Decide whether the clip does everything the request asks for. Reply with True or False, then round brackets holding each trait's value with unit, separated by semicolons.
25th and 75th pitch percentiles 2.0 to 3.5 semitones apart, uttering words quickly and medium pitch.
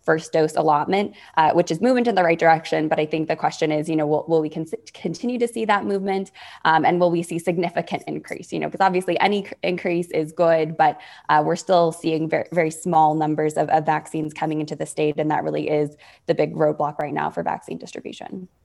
True (2.5 semitones; 225 wpm; 160 Hz)